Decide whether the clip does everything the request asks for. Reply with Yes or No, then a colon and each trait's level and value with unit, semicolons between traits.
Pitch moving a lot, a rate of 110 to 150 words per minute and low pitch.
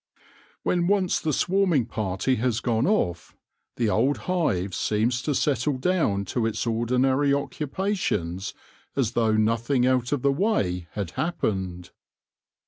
Yes: wide, 5.7 semitones; slow, 135 wpm; low, 125 Hz